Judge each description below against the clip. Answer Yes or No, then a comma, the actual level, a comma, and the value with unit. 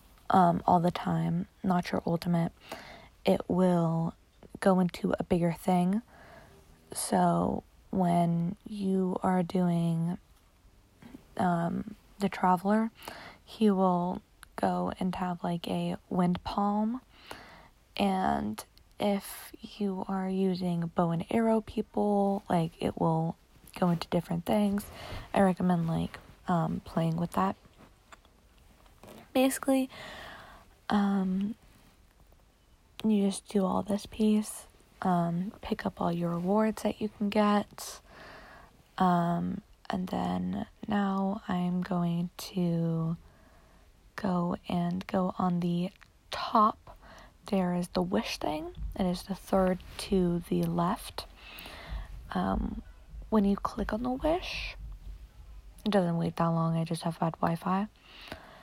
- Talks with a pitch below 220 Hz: Yes, medium, 185 Hz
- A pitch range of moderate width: Yes, average, 3.0 semitones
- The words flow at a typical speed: No, fast, 115 wpm